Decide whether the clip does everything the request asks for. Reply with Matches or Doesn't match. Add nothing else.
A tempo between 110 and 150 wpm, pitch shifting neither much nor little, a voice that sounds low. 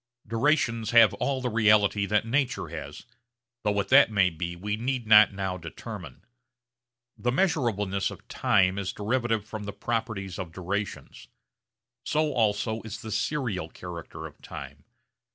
Matches